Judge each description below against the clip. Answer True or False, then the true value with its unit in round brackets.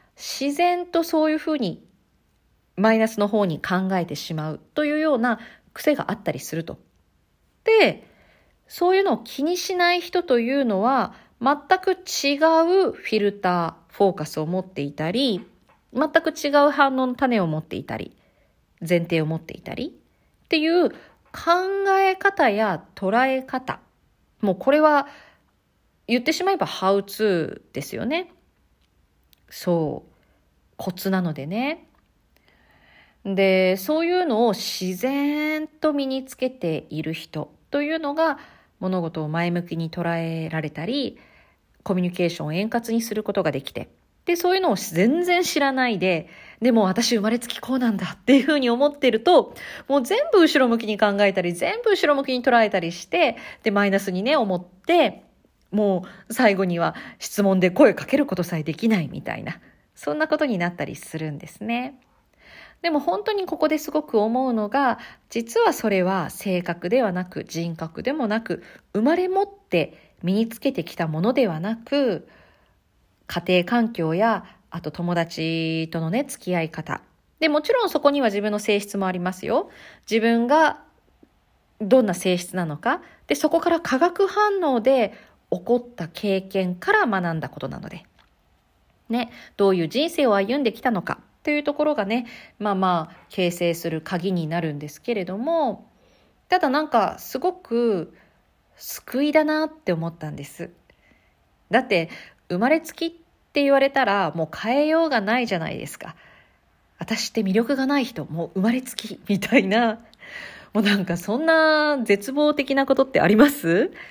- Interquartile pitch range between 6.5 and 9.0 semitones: True (8.3 semitones)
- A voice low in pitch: False (220 Hz)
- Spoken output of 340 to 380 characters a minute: False (300 characters per minute)